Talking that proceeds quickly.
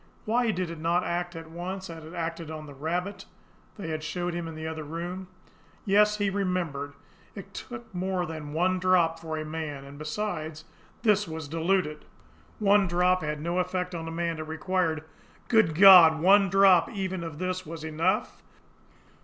No: average, 180 wpm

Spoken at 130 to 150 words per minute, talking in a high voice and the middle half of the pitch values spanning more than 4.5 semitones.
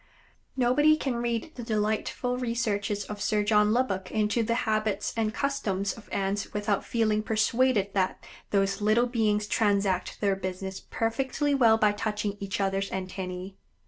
No: average, 145 wpm; high, 210 Hz; average, 2.8 semitones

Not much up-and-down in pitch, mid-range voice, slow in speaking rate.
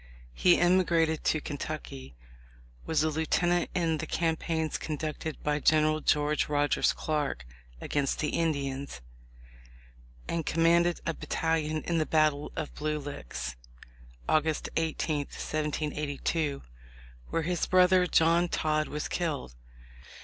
Yes: narrow, 1.9 semitones; medium, 155 Hz; slow, 120 wpm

